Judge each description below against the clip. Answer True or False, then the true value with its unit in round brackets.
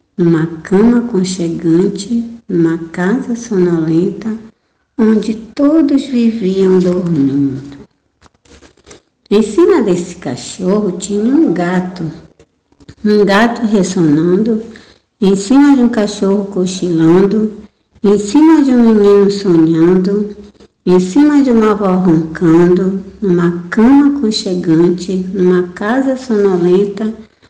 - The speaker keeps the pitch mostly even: False (3.9 semitones)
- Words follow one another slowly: True (95 wpm)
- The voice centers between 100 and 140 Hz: False (195 Hz)